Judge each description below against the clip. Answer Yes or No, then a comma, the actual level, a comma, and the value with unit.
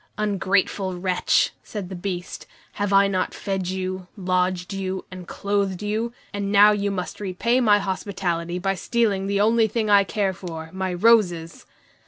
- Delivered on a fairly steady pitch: Yes, narrow, 2.0 semitones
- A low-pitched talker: No, high, 195 Hz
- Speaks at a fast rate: No, average, 160 wpm